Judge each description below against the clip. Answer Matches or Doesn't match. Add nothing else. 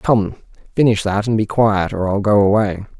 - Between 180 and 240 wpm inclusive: Matches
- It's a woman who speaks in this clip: Doesn't match